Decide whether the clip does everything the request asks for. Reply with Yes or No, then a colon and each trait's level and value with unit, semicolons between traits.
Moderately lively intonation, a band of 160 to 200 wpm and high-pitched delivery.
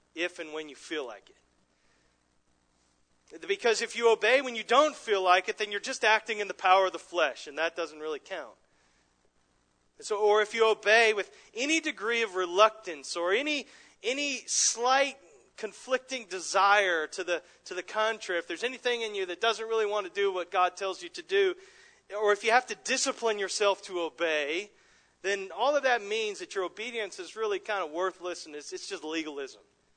No: wide, 6.2 semitones; average, 195 wpm; high, 205 Hz